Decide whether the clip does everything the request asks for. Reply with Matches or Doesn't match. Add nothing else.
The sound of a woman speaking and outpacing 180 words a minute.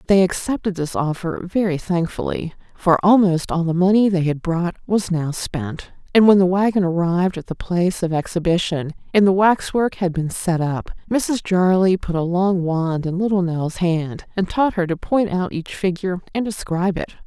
Matches